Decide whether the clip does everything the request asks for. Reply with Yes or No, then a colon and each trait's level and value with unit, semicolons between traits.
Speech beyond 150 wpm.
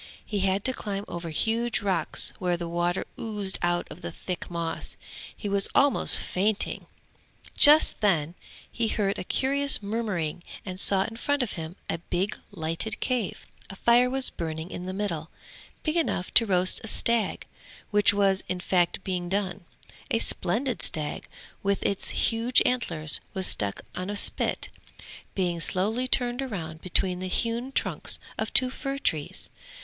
Yes: average, 160 wpm